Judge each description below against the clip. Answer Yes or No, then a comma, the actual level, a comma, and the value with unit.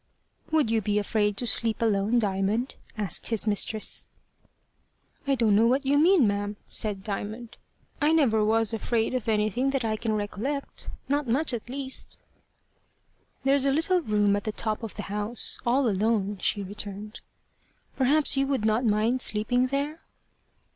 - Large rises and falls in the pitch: No, average, 4.2 semitones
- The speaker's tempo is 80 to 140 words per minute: No, average, 160 wpm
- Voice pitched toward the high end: Yes, high, 225 Hz